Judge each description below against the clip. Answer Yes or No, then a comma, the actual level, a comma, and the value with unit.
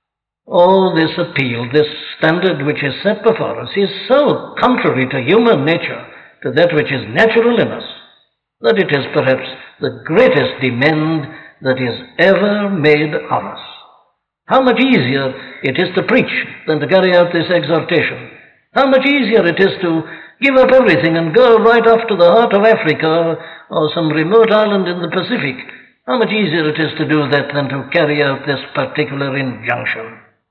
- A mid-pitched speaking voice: Yes, medium, 165 Hz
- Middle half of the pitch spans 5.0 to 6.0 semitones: Yes, wide, 5.6 semitones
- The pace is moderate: Yes, average, 175 wpm